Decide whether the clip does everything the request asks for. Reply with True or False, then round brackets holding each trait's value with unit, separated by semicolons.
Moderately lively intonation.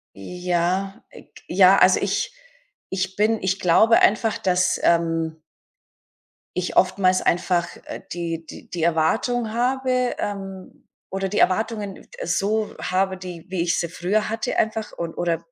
True (3.6 semitones)